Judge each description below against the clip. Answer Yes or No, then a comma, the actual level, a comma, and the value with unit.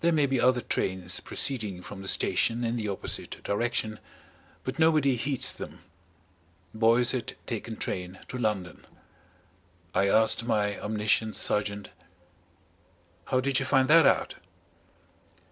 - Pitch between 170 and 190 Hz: No, low, 115 Hz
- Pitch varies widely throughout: No, average, 4.0 semitones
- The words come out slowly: Yes, slow, 130 wpm